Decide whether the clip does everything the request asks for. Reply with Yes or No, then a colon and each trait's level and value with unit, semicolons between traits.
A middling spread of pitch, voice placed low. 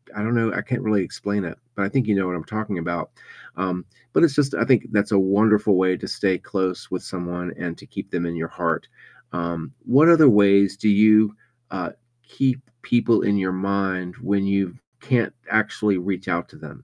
Yes: average, 3.1 semitones; low, 100 Hz